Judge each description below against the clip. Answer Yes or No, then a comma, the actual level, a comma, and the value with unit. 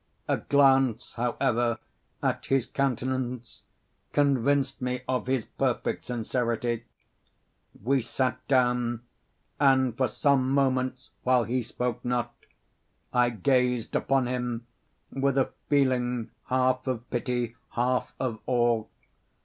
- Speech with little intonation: Yes, narrow, 1.6 semitones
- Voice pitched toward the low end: Yes, low, 125 Hz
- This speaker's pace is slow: Yes, slow, 110 wpm